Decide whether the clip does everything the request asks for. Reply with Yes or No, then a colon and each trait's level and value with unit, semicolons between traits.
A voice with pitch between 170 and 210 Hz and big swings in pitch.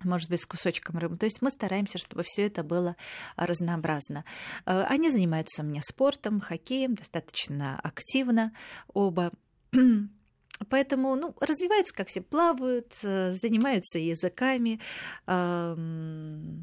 Yes: high, 190 Hz; wide, 6.6 semitones